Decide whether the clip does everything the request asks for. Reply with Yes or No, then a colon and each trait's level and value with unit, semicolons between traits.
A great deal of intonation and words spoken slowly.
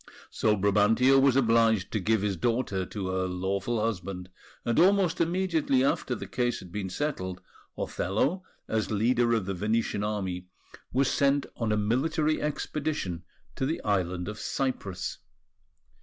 No: wide, 5.7 semitones; average, 145 wpm